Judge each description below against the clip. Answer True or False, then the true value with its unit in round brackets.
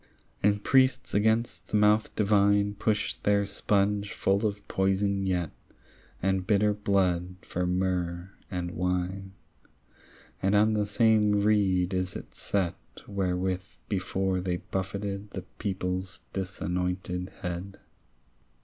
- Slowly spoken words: True (115 wpm)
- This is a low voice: True (95 Hz)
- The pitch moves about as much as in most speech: False (2.0 semitones)